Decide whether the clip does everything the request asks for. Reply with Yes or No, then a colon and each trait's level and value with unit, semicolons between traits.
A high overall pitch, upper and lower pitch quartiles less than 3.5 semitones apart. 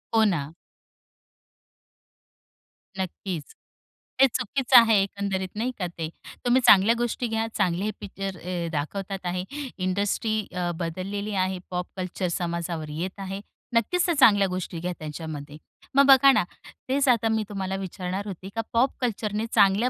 No: high, 195 Hz; average, 3.8 semitones